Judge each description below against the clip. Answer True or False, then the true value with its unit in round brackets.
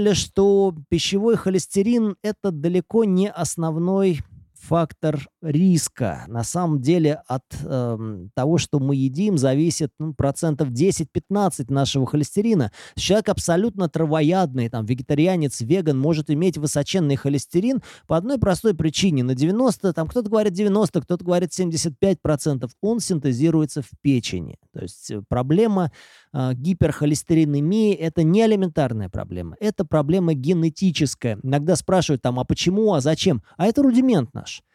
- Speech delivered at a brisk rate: False (130 wpm)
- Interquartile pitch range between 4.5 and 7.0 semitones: True (5.1 semitones)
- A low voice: False (165 Hz)